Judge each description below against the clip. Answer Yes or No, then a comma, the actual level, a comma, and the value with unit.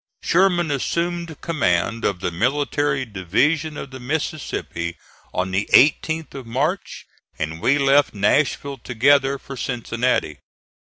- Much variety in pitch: Yes, wide, 5.7 semitones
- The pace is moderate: No, slow, 120 wpm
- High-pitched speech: No, low, 135 Hz